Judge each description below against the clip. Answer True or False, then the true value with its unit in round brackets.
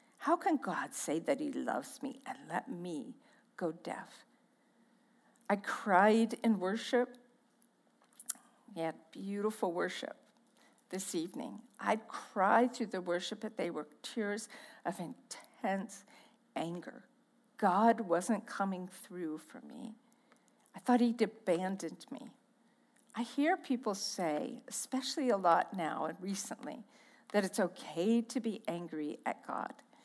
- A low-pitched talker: False (230 Hz)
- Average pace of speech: False (130 wpm)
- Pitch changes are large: False (4.3 semitones)